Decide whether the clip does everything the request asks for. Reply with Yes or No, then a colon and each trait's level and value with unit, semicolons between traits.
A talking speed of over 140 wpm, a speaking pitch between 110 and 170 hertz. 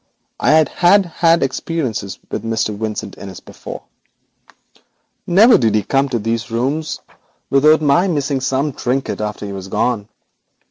Yes: average, 150 wpm; low, 135 Hz